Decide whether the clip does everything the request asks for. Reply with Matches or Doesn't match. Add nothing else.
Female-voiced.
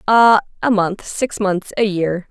Matches